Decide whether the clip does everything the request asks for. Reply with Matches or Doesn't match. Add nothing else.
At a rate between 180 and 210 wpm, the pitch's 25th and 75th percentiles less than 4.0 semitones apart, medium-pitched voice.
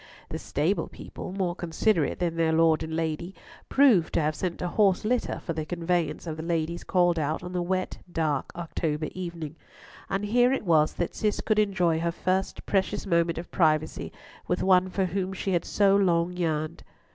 Matches